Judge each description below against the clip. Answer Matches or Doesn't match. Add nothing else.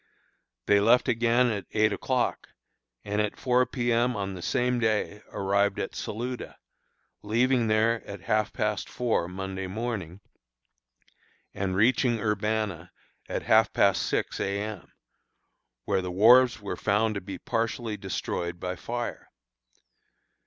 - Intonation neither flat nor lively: Matches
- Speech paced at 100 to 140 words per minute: Matches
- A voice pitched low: Matches